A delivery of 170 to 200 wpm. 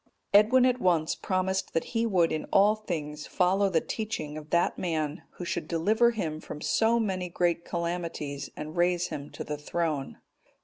Yes: average, 175 wpm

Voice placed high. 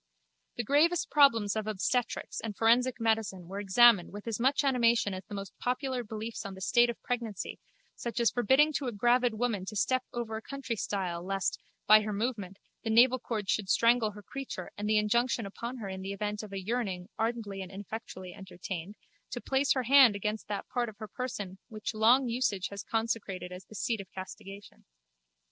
Yes: high, 220 Hz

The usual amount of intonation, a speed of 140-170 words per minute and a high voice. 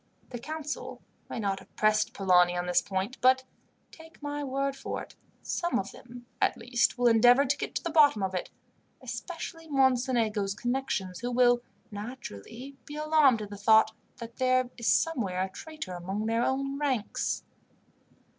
Yes: average, 5.0 semitones; average, 165 wpm; high, 245 Hz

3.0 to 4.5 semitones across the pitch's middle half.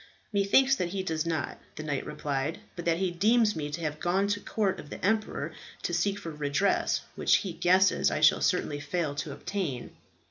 No: average, 4.9 semitones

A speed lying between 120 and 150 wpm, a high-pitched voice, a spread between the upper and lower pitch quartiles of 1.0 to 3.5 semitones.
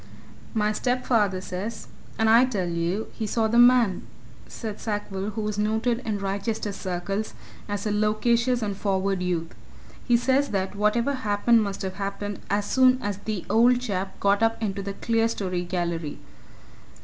No: average, 160 wpm; high, 210 Hz; average, 2.8 semitones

